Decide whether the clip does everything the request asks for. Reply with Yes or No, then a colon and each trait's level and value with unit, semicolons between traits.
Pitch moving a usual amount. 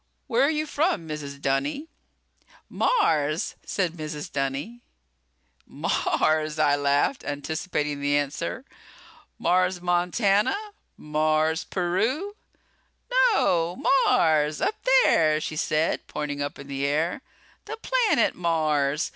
No: wide, 5.9 semitones